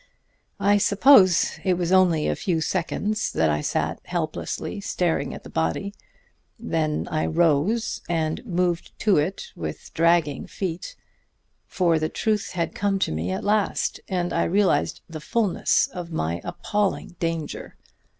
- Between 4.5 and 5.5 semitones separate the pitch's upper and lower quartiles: No, average, 4.0 semitones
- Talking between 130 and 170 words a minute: Yes, average, 150 wpm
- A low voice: No, medium, 175 Hz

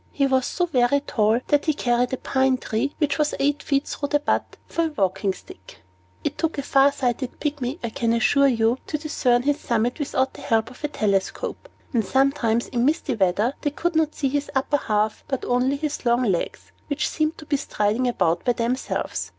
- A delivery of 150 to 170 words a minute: No, fast, 205 wpm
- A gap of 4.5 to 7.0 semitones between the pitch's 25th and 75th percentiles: No, average, 3.7 semitones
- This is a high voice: Yes, very high, 260 Hz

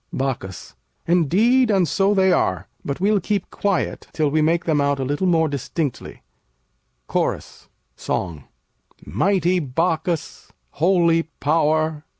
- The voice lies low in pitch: No, medium, 165 Hz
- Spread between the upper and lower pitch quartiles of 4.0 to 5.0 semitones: Yes, average, 4.4 semitones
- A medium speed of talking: No, slow, 125 wpm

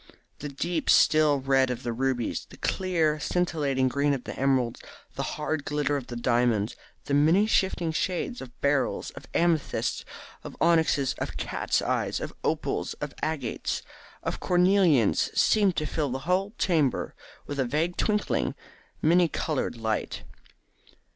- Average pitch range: Yes, average, 4.4 semitones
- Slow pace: No, average, 145 wpm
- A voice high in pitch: No, medium, 150 Hz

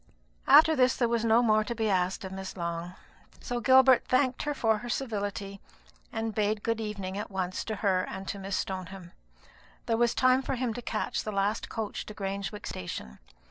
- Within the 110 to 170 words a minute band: No, average, 195 wpm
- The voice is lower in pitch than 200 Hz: No, high, 215 Hz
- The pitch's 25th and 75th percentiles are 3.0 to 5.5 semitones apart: Yes, average, 3.6 semitones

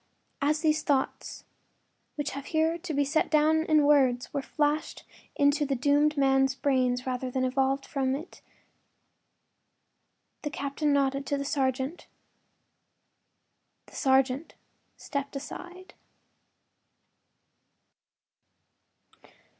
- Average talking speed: No, slow, 105 wpm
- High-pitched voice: Yes, very high, 280 Hz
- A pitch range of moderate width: No, narrow, 2.1 semitones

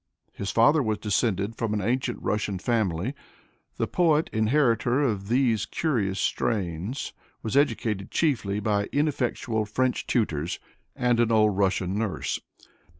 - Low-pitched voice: Yes, low, 110 Hz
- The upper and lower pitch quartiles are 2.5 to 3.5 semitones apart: No, average, 4.0 semitones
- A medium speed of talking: No, slow, 130 wpm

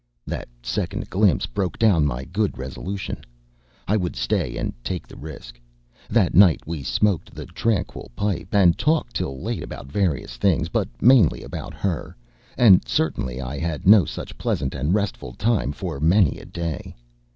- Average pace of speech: Yes, average, 165 wpm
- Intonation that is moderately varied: No, wide, 6.2 semitones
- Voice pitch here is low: Yes, very low, 85 Hz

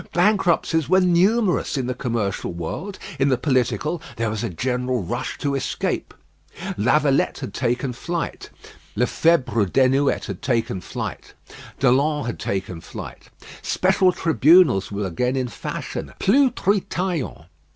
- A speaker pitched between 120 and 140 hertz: Yes, low, 135 Hz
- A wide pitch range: Yes, wide, 6.3 semitones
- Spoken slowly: Yes, slow, 130 wpm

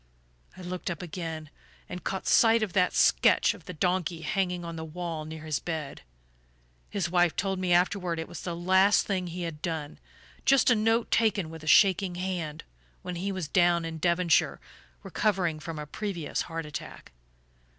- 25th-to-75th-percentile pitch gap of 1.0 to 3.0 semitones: Yes, narrow, 2.6 semitones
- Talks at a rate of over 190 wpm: No, average, 180 wpm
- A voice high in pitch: No, medium, 175 Hz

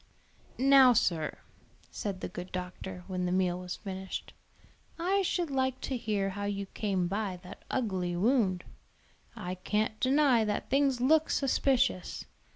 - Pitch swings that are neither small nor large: No, wide, 6.1 semitones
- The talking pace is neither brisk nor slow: Yes, average, 145 wpm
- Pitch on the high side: Yes, high, 205 Hz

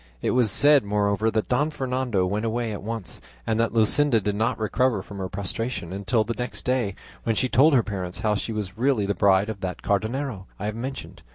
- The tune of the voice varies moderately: Yes, average, 3.6 semitones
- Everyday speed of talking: No, fast, 215 wpm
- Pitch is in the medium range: No, low, 110 Hz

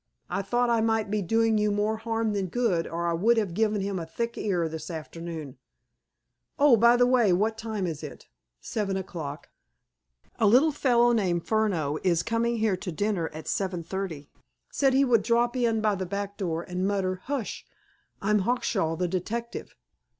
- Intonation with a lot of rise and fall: No, average, 4.4 semitones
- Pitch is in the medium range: No, high, 205 Hz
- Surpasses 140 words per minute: Yes, average, 180 wpm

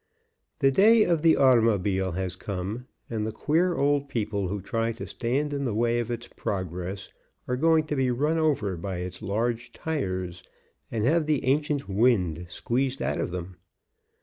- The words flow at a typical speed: Yes, average, 175 wpm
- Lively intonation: Yes, wide, 6.7 semitones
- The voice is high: No, low, 115 Hz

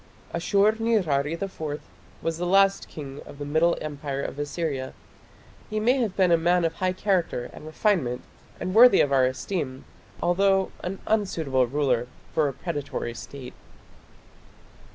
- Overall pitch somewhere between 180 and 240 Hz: No, medium, 165 Hz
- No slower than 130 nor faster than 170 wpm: Yes, average, 150 wpm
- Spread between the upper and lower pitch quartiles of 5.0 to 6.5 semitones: Yes, wide, 5.5 semitones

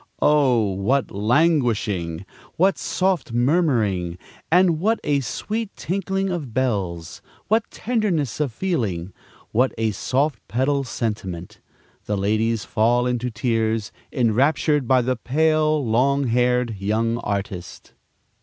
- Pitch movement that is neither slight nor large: No, wide, 5.9 semitones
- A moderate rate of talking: No, slow, 115 wpm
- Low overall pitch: Yes, low, 125 Hz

